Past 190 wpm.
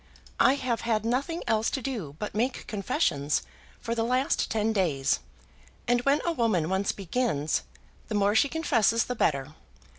No: average, 160 wpm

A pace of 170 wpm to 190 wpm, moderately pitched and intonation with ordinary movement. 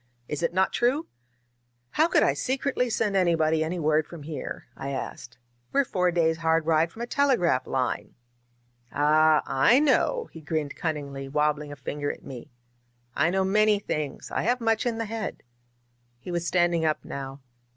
No: average, 175 wpm; medium, 165 Hz; wide, 6.2 semitones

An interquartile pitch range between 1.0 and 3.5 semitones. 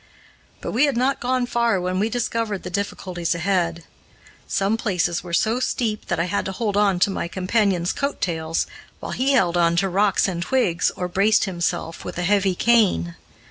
No: average, 4.4 semitones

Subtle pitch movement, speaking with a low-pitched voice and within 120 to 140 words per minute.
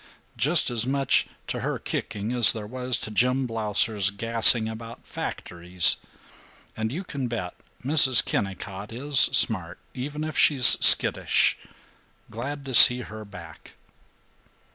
No: average, 3.8 semitones; low, 115 Hz; slow, 135 wpm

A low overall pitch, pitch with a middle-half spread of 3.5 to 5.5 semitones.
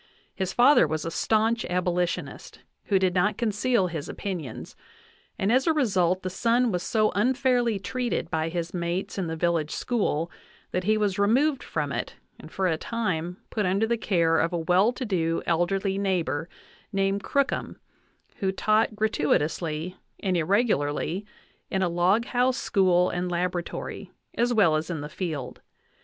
No: high, 190 Hz; average, 4.2 semitones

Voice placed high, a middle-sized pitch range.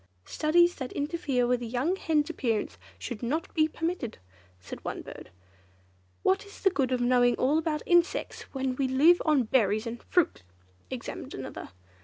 Yes: very high, 270 Hz; average, 5.0 semitones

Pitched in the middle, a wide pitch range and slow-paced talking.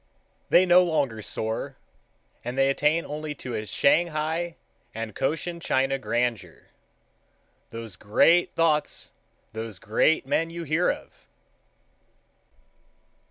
Yes: medium, 145 Hz; wide, 6.1 semitones; slow, 125 wpm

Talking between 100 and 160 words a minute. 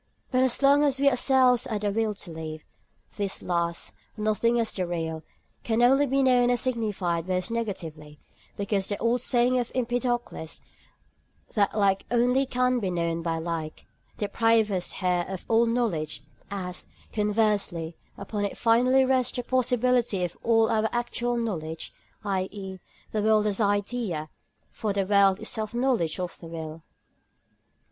Yes: average, 155 wpm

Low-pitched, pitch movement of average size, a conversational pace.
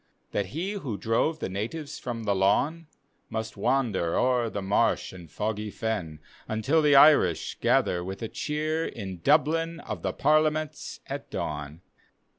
No: low, 115 Hz; wide, 7.8 semitones; average, 150 wpm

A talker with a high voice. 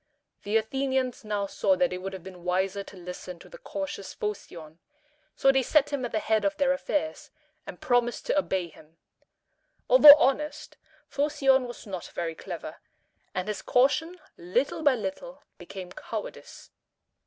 Yes: high, 245 Hz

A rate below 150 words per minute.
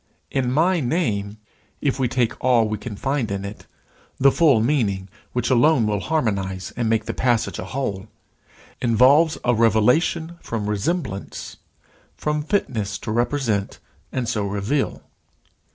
Yes: average, 140 wpm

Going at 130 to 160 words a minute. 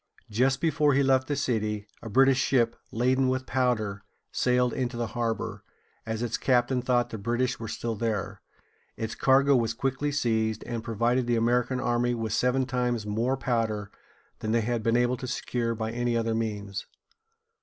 No: average, 175 wpm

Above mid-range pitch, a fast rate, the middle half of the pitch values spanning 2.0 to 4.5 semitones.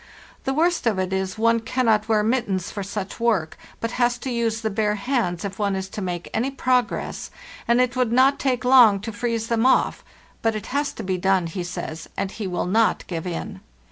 Yes: high, 220 Hz; fast, 215 wpm; average, 4.2 semitones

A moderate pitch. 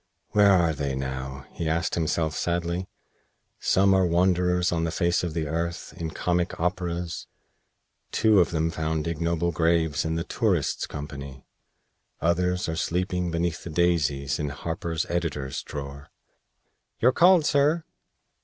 No: very low, 85 Hz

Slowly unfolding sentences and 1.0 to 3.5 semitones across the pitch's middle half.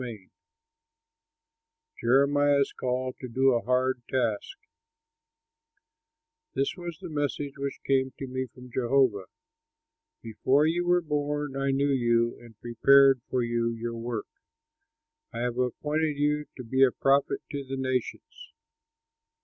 Yes: slow, 130 wpm; average, 2.9 semitones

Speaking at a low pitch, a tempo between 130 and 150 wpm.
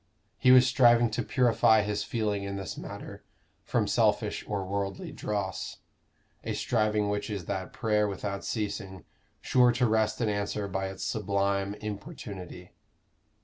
Yes: low, 105 Hz; average, 145 wpm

